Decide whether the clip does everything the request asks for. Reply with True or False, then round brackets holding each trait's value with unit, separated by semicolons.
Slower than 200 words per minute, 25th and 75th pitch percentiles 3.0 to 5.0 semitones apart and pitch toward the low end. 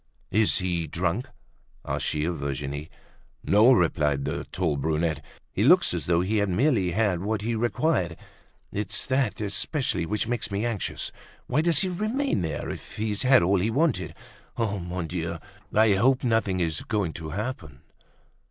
False (160 wpm; 5.5 semitones; 100 Hz)